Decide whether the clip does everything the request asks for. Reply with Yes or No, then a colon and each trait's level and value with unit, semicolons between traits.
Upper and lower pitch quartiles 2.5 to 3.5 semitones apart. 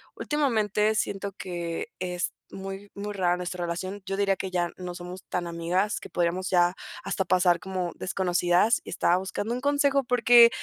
Yes: average, 2.8 semitones